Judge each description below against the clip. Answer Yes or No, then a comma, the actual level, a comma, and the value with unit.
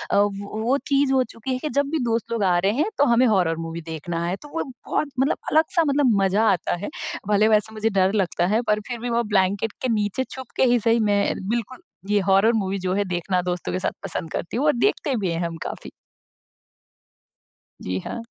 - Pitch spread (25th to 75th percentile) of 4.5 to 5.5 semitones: Yes, average, 5.0 semitones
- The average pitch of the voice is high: Yes, high, 215 Hz